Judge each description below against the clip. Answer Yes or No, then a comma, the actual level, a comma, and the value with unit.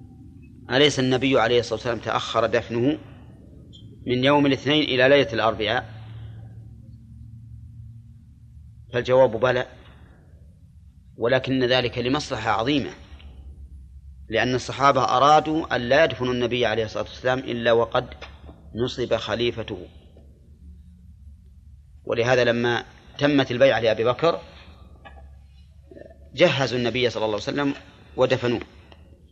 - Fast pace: No, average, 95 wpm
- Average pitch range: No, wide, 7.4 semitones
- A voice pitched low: Yes, low, 115 Hz